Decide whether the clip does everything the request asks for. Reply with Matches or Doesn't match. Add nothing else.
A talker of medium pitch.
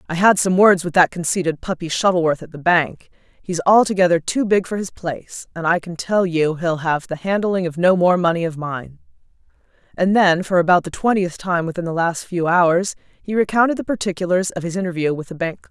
Matches